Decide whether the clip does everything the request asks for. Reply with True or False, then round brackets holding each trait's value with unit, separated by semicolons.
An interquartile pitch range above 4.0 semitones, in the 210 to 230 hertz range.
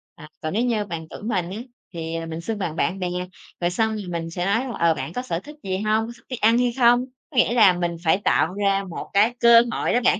False (5.2 semitones; 195 Hz)